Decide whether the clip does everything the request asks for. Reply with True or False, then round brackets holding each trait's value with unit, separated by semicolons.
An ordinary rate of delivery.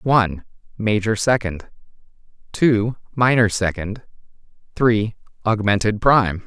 False (85 wpm)